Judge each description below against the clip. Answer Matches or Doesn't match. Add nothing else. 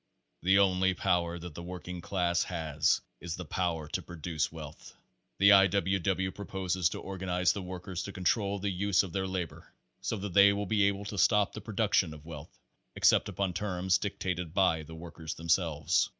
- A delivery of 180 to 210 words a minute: Matches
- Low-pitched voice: Matches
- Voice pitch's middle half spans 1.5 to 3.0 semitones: Matches